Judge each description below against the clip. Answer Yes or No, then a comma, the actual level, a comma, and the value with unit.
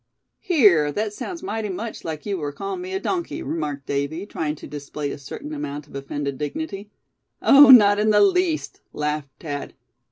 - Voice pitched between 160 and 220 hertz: Yes, medium, 185 Hz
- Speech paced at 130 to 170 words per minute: No, average, 180 wpm